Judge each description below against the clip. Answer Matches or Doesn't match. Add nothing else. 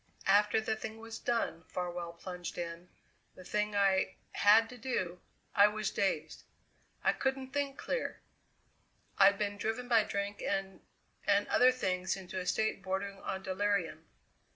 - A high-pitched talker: Matches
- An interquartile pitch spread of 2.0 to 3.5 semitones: Matches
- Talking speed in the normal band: Matches